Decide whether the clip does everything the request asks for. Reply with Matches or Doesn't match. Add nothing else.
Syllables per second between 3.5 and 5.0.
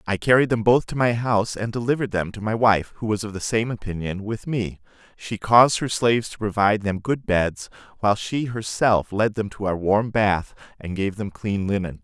Doesn't match